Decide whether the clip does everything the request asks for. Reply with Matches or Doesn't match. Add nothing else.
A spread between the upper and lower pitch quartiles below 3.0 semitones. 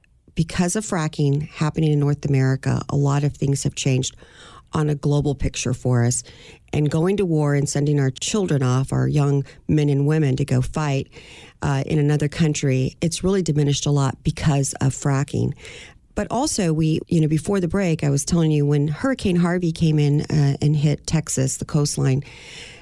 Matches